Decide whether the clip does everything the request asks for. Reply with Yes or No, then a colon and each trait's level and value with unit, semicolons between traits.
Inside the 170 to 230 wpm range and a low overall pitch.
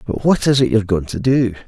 No: fast, 285 wpm; low, 115 Hz